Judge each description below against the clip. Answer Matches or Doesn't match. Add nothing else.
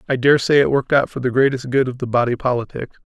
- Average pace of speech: Doesn't match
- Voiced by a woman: Doesn't match